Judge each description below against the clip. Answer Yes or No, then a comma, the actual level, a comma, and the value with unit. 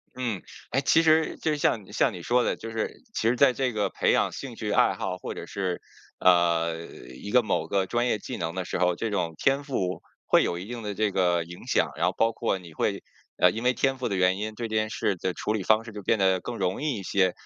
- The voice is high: No, low, 105 Hz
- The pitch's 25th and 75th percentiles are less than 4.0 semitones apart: No, average, 4.6 semitones